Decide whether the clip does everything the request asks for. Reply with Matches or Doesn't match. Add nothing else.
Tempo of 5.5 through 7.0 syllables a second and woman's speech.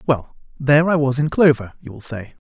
Doesn't match